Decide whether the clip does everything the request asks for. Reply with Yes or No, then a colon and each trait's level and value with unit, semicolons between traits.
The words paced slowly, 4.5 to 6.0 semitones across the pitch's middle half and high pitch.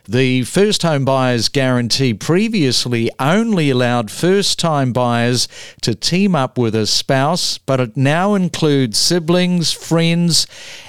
No: slow, 125 wpm; wide, 5.5 semitones; low, 135 Hz